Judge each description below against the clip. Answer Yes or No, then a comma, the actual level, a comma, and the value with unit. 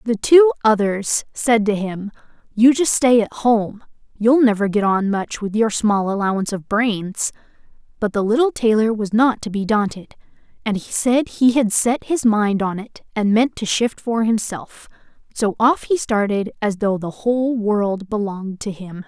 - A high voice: Yes, high, 220 Hz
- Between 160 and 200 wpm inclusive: Yes, average, 180 wpm